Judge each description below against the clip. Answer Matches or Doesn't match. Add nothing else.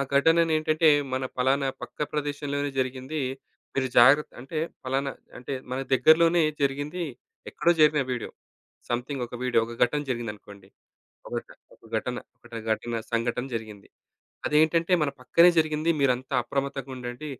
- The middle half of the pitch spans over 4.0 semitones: Doesn't match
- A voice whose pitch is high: Doesn't match